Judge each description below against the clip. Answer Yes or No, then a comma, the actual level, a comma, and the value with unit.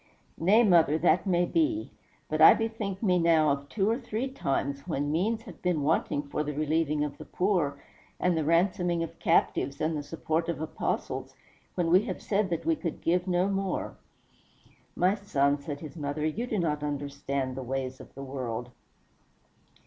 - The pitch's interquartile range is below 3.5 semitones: No, average, 4.8 semitones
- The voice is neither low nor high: Yes, medium, 165 Hz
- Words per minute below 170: No, average, 180 wpm